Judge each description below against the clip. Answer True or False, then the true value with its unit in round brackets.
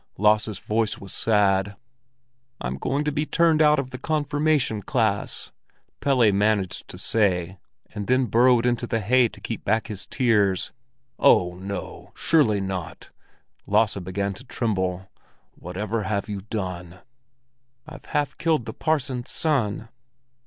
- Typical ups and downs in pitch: True (4.6 semitones)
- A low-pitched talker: True (110 Hz)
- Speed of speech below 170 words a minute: True (135 wpm)